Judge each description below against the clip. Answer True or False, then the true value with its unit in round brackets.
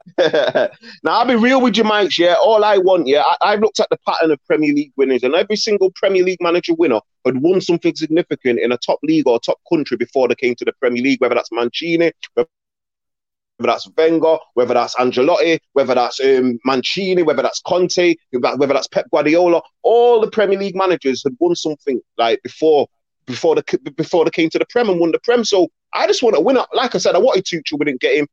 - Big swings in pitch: True (6.0 semitones)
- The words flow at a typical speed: False (220 wpm)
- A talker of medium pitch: True (175 Hz)